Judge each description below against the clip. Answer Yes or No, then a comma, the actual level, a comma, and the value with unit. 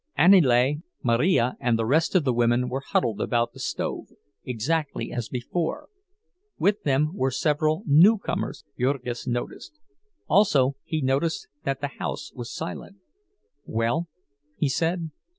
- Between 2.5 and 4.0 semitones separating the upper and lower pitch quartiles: No, average, 5.0 semitones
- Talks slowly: Yes, slow, 130 wpm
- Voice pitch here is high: No, medium, 140 Hz